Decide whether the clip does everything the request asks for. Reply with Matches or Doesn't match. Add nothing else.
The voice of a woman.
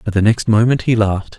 Doesn't match